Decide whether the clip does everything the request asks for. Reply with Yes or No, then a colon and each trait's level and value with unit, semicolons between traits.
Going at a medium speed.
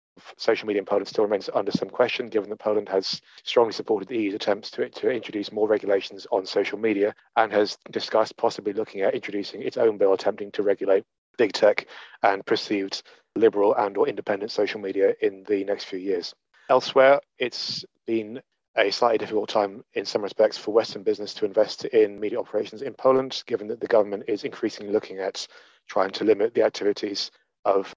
Yes: average, 190 wpm